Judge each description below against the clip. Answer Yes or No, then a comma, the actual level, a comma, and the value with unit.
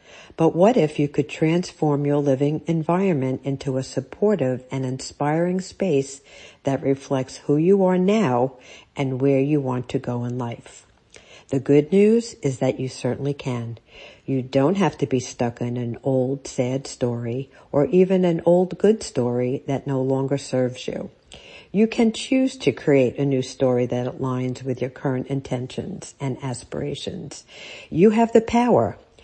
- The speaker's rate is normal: Yes, average, 160 wpm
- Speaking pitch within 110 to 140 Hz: Yes, low, 135 Hz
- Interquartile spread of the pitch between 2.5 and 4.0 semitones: No, average, 4.4 semitones